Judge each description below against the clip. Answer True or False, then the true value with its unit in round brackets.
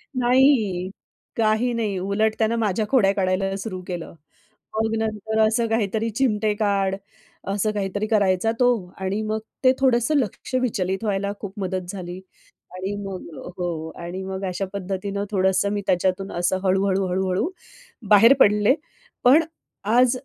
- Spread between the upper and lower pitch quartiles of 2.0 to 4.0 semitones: True (2.7 semitones)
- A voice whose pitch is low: False (200 Hz)